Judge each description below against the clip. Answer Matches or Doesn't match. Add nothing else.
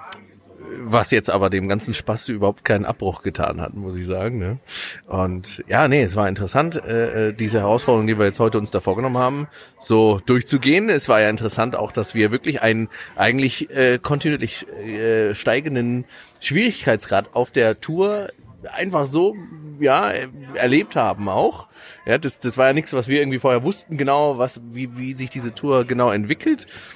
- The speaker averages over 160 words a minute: Matches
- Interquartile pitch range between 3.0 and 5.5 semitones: Matches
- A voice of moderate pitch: Doesn't match